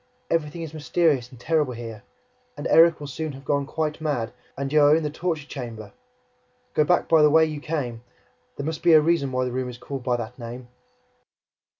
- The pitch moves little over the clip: No, average, 4.0 semitones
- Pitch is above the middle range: No, medium, 145 Hz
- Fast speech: Yes, fast, 210 wpm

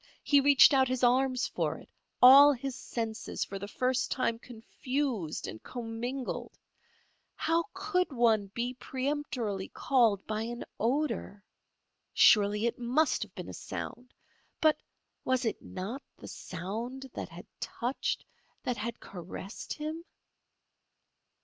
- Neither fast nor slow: No, slow, 125 wpm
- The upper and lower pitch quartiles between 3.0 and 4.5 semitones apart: Yes, average, 3.6 semitones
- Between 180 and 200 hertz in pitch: No, high, 245 Hz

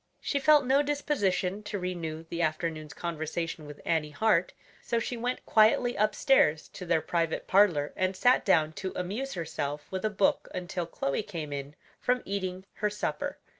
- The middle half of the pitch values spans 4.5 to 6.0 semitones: Yes, average, 5.0 semitones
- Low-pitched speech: No, medium, 185 Hz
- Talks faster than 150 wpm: Yes, average, 170 wpm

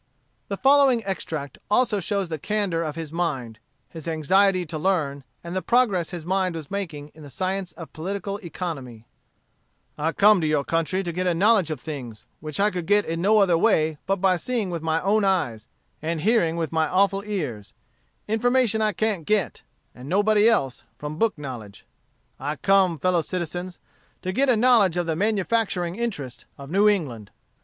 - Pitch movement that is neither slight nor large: Yes, average, 4.5 semitones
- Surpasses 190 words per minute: No, average, 180 wpm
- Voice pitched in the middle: Yes, medium, 180 Hz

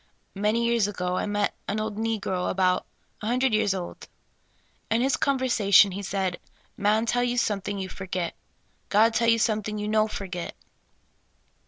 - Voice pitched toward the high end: Yes, high, 210 Hz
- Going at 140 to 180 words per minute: Yes, average, 170 wpm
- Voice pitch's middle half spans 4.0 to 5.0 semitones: No, average, 2.7 semitones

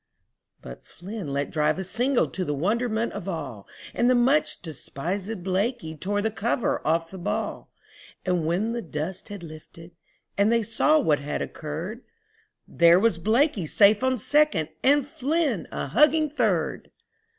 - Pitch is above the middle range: Yes, high, 200 Hz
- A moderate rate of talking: Yes, average, 155 wpm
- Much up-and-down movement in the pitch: Yes, wide, 6.3 semitones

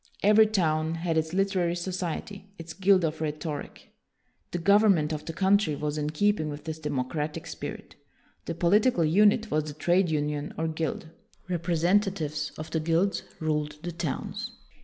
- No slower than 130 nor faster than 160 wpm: Yes, average, 155 wpm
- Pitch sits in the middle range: Yes, medium, 165 Hz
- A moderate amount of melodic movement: Yes, average, 3.7 semitones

